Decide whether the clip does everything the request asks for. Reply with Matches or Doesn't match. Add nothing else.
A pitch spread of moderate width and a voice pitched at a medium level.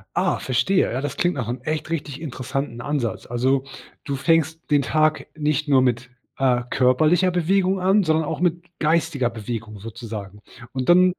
Matches